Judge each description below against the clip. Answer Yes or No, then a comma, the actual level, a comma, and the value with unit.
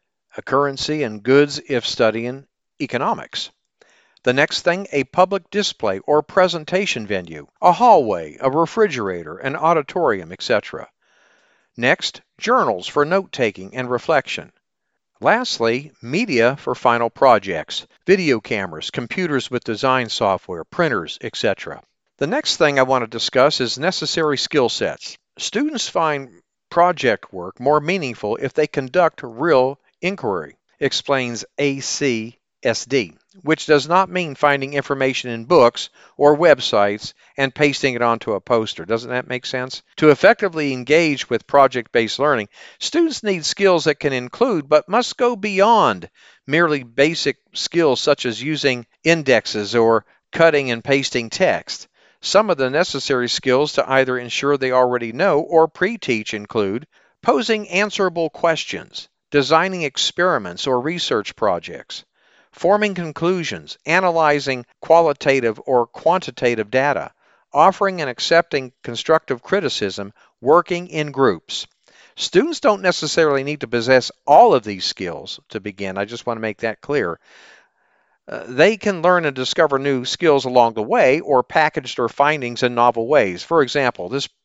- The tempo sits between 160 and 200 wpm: No, average, 140 wpm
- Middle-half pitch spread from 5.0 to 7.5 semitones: Yes, average, 5.3 semitones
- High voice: No, medium, 140 Hz